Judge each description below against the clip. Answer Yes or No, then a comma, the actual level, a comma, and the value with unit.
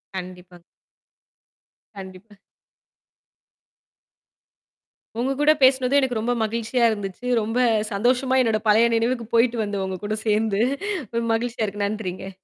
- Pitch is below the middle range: No, high, 220 Hz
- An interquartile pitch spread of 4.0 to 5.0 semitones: No, average, 3.4 semitones